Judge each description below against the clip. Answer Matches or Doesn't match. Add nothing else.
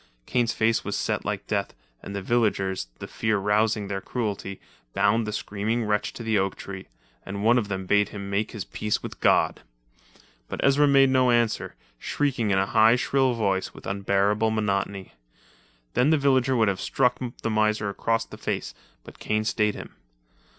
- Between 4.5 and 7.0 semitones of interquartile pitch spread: Doesn't match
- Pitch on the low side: Matches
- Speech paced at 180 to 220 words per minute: Matches